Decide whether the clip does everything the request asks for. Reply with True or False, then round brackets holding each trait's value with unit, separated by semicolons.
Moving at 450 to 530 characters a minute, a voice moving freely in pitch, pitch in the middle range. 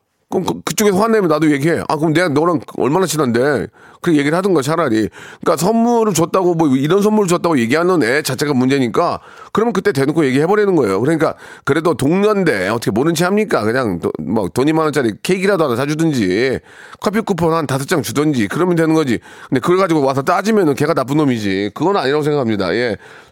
False (455 characters per minute; 4.6 semitones; 160 Hz)